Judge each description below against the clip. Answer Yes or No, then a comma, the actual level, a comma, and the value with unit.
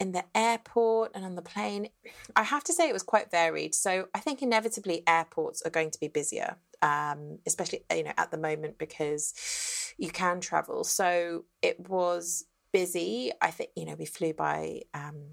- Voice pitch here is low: No, medium, 175 Hz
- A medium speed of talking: Yes, average, 190 wpm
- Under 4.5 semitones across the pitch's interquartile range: No, wide, 5.5 semitones